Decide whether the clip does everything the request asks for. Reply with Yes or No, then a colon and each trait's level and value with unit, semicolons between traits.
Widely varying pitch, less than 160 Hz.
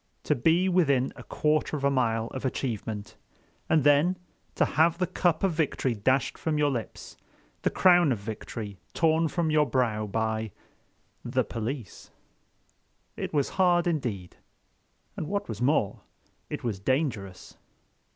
Yes: wide, 6.0 semitones; low, 135 Hz